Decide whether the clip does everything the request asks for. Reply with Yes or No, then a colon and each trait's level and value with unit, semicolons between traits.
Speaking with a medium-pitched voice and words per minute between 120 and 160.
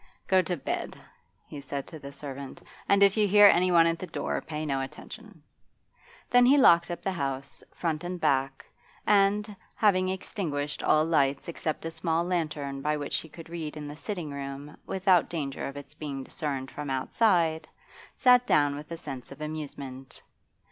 No: medium, 155 Hz; average, 175 wpm